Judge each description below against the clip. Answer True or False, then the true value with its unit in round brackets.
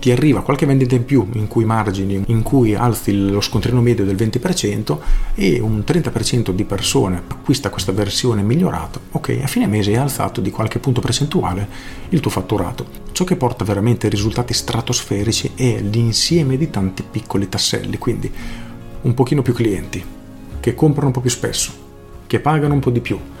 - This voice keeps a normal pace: False (175 wpm)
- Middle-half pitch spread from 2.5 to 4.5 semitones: True (3.9 semitones)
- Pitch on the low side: True (115 Hz)